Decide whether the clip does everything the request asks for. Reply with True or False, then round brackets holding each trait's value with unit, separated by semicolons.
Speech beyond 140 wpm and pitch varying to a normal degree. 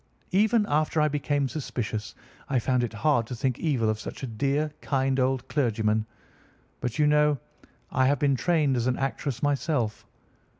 True (170 wpm; 3.6 semitones)